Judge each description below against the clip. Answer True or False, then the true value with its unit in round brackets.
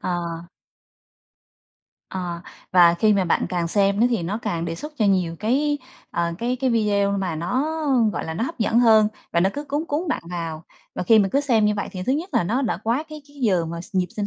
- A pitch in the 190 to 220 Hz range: True (205 Hz)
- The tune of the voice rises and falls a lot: True (5.7 semitones)